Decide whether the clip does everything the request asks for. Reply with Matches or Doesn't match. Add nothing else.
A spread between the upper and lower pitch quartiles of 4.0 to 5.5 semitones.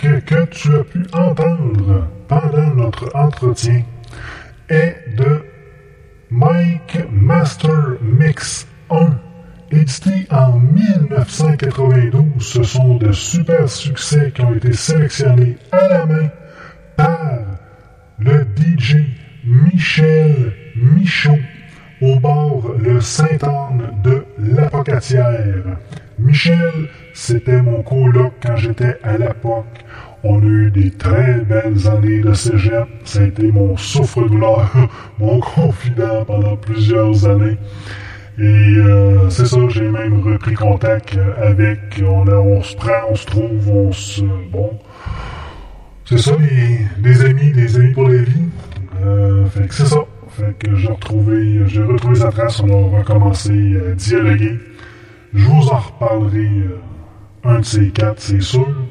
Matches